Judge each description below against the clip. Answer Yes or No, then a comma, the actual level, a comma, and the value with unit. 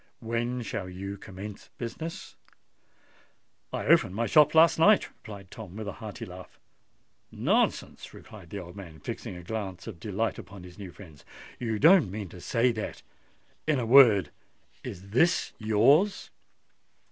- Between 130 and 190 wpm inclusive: Yes, average, 145 wpm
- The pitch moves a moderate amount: Yes, average, 4.3 semitones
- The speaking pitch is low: Yes, low, 105 Hz